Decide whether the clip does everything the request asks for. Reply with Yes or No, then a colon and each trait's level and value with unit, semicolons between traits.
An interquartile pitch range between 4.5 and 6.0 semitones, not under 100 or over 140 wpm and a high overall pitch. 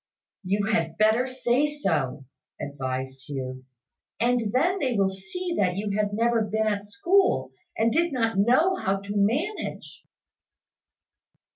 Yes: average, 5.1 semitones; slow, 135 wpm; high, 215 Hz